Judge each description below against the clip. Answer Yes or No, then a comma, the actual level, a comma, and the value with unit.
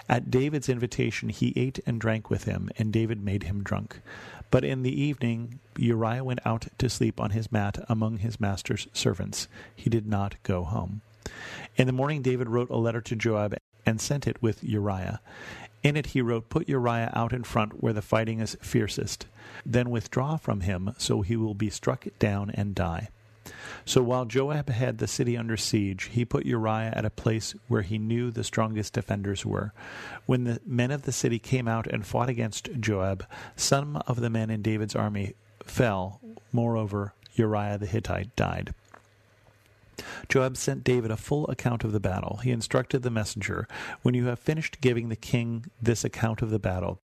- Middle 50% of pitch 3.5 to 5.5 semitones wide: No, average, 2.8 semitones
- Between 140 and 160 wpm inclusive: No, average, 185 wpm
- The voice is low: Yes, low, 115 Hz